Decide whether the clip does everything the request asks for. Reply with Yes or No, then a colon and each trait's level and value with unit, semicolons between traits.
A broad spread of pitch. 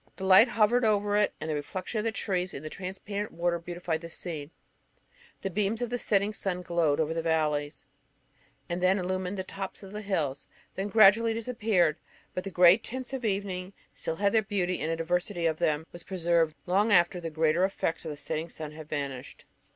No: average, 3.9 semitones